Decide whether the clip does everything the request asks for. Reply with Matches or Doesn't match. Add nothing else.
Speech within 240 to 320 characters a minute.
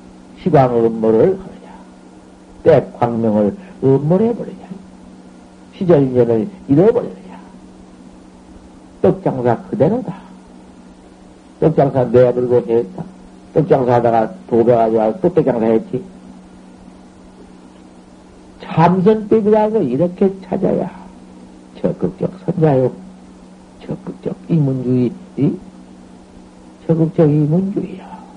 Doesn't match